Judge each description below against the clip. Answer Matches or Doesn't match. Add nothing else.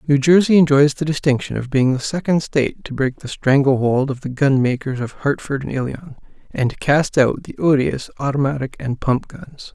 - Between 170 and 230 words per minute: Matches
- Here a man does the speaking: Matches